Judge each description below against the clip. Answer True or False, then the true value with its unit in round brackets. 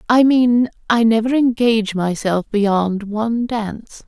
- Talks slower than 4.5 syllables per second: True (4.0 syllables/s)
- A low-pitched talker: False (225 Hz)